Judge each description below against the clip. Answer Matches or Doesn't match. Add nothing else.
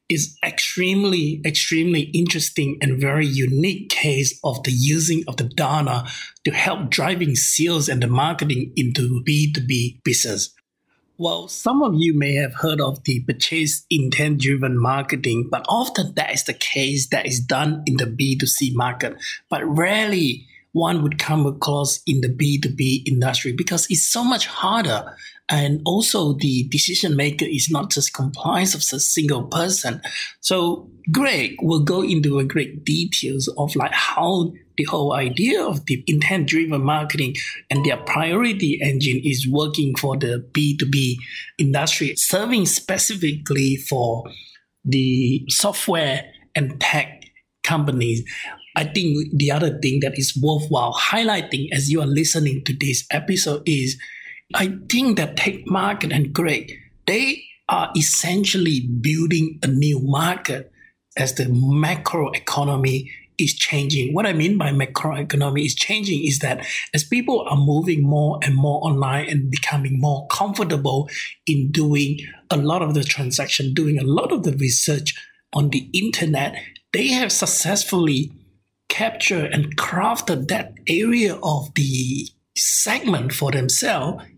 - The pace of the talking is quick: Doesn't match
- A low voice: Doesn't match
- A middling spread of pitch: Matches